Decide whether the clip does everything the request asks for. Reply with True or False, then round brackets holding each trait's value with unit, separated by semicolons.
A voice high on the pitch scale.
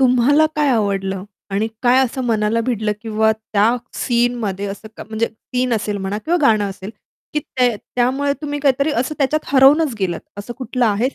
True (235 Hz)